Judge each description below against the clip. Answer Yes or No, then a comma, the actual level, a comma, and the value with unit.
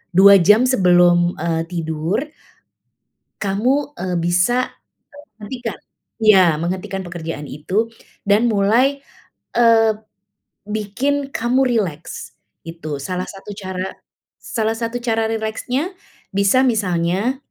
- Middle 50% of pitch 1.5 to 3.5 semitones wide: No, average, 4.8 semitones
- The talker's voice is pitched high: Yes, high, 205 Hz